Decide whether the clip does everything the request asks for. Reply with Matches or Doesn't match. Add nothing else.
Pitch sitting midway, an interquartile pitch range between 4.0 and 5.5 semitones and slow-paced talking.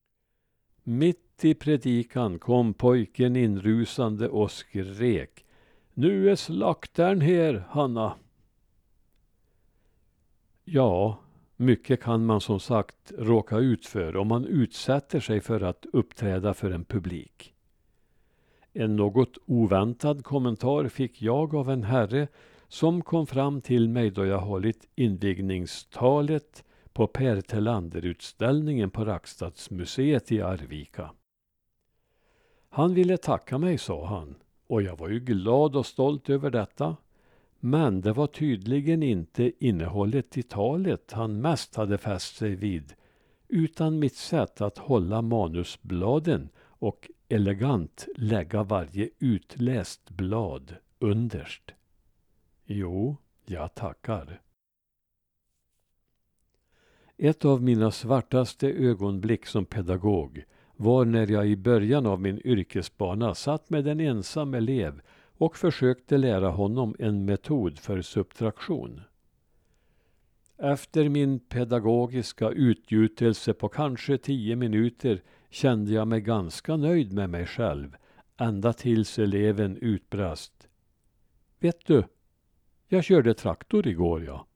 Doesn't match